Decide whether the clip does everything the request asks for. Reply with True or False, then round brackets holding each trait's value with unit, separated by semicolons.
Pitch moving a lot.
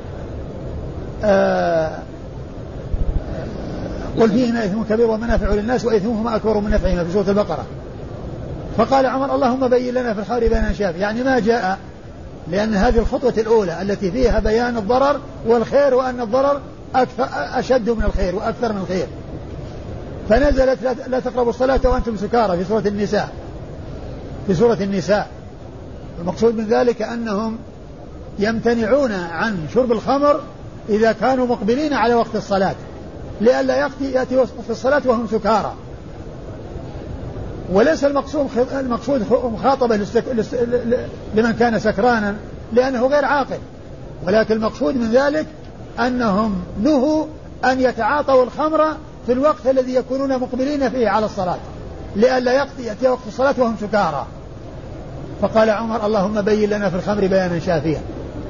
False (3.8 semitones)